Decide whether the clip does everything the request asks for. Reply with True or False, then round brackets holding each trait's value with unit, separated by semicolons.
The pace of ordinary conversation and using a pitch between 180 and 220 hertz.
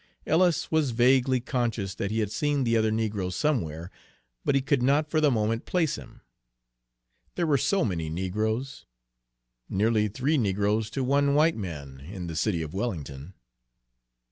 False (160 wpm; 115 Hz)